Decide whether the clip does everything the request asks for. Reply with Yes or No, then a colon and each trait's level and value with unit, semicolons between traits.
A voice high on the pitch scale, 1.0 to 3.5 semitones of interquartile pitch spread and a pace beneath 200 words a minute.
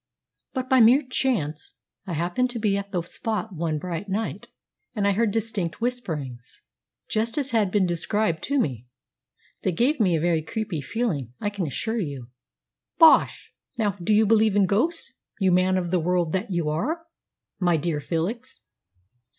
No: high, 195 Hz; average, 5.1 semitones; average, 170 wpm